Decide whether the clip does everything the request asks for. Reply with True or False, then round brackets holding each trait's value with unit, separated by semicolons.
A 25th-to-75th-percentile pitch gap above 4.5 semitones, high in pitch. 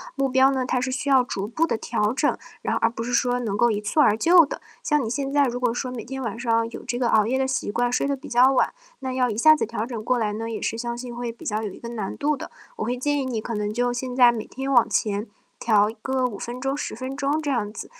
False (2.7 semitones; 245 Hz)